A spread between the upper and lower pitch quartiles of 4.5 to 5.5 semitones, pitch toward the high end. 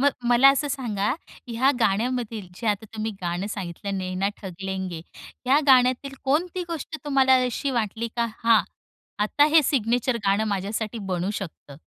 Yes: average, 5.0 semitones; high, 225 Hz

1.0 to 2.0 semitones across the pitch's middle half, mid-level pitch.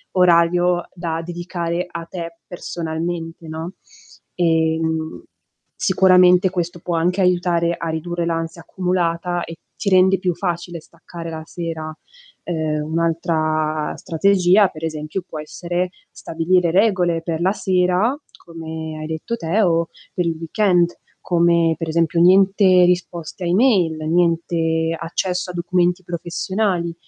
Yes: narrow, 1.7 semitones; medium, 170 Hz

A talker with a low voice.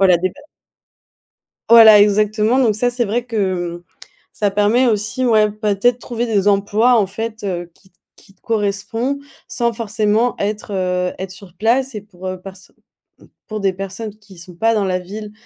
No: high, 210 Hz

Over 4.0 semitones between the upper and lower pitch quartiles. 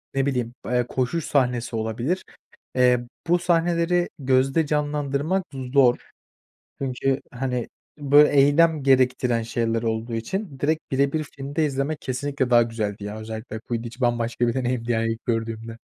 No: average, 3.6 semitones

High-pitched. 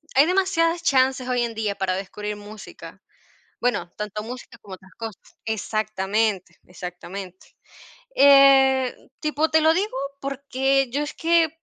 Yes: high, 245 Hz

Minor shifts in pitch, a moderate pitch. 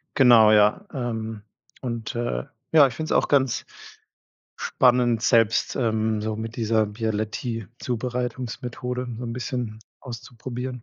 No: narrow, 2.3 semitones; low, 120 Hz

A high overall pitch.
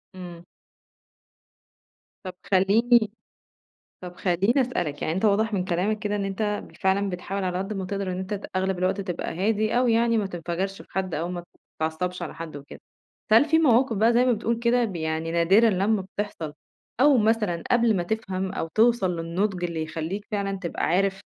Yes: high, 195 Hz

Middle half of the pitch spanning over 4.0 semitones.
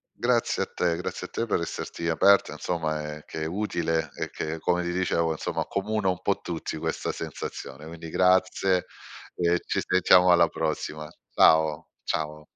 No: narrow, 2.5 semitones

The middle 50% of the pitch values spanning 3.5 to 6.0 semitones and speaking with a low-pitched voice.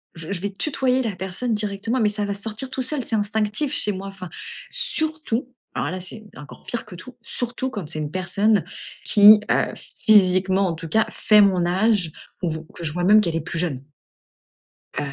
No: average, 3.8 semitones; high, 205 Hz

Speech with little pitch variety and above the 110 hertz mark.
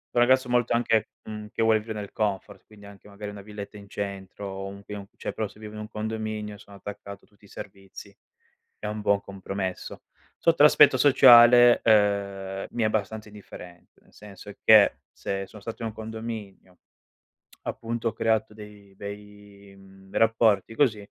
No: narrow, 1.7 semitones; low, 105 Hz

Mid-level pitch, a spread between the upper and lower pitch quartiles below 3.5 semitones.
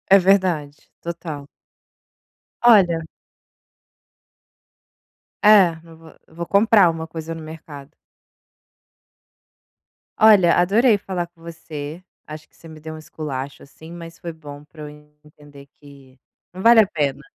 Yes: medium, 165 Hz; average, 3.0 semitones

